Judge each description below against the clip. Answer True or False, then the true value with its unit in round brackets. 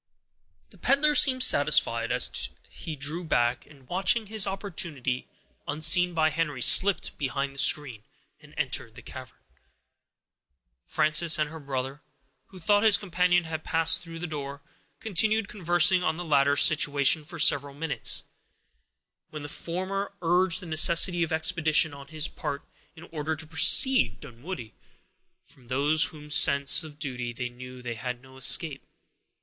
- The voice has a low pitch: False (155 Hz)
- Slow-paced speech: False (145 wpm)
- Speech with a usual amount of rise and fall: True (3.9 semitones)